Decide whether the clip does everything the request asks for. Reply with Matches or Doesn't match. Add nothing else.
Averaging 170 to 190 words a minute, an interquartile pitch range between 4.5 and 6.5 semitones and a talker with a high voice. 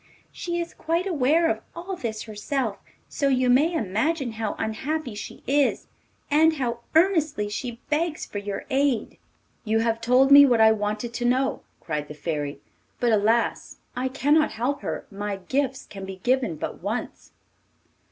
Doesn't match